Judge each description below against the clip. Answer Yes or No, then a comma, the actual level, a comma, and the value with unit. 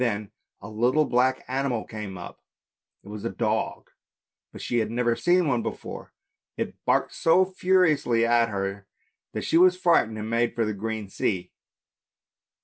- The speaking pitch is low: Yes, low, 115 Hz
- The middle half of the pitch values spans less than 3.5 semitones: No, average, 4.7 semitones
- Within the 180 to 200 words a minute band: No, average, 160 wpm